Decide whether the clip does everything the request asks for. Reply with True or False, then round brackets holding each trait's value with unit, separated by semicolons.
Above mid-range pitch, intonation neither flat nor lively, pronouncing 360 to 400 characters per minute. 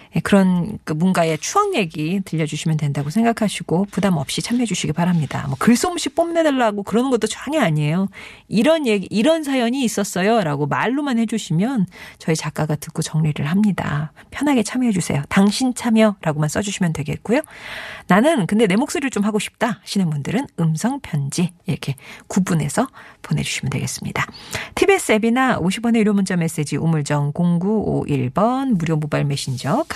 False (200 Hz; 6.3 semitones; 365 characters per minute)